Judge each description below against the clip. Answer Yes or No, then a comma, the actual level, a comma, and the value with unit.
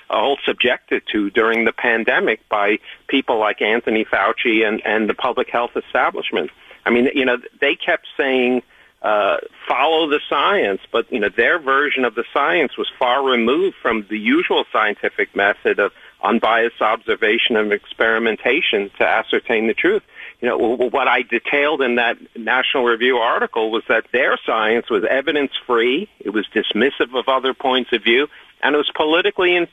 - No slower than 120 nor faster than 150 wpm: No, average, 170 wpm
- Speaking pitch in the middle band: Yes, medium, 175 Hz